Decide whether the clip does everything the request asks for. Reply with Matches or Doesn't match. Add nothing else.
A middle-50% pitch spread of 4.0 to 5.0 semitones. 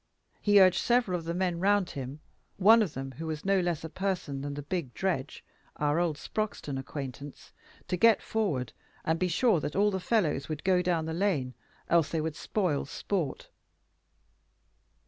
Matches